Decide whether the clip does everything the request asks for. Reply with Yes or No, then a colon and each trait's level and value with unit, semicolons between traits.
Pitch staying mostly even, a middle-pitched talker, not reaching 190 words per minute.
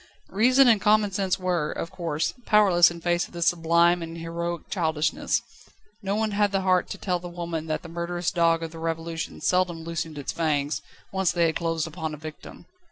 No: narrow, 2.1 semitones; medium, 170 Hz; fast, 205 wpm